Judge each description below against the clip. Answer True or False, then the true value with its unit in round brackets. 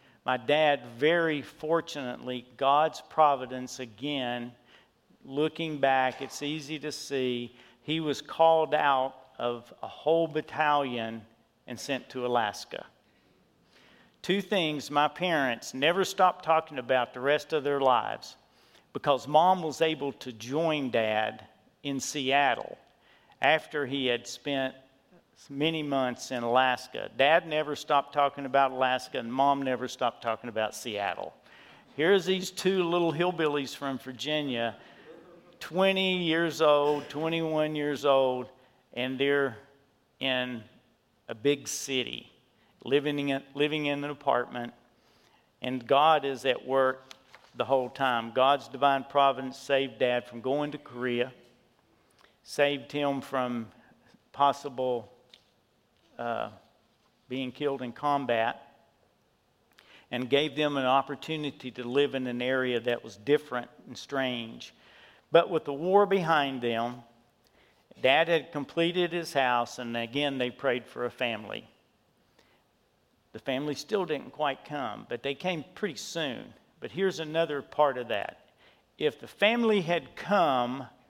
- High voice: False (140 Hz)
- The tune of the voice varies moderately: True (3.3 semitones)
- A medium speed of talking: False (130 wpm)